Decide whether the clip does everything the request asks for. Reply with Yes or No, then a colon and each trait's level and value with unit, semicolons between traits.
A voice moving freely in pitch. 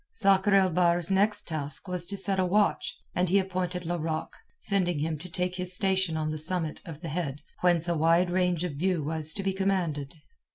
No: average, 2.8 semitones